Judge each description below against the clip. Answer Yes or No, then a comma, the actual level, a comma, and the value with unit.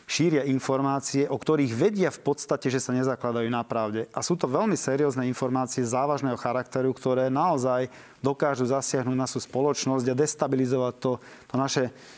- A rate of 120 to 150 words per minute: No, average, 160 wpm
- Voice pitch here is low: Yes, low, 130 Hz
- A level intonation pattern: Yes, narrow, 1.6 semitones